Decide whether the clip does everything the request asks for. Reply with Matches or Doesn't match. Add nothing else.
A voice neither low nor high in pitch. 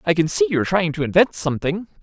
Matches